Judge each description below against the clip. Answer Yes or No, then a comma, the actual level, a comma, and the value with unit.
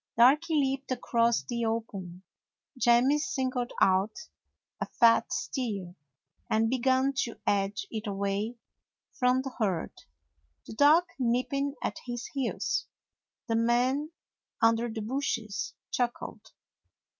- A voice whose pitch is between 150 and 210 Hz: No, high, 240 Hz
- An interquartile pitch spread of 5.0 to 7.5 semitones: No, average, 3.3 semitones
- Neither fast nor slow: No, slow, 115 wpm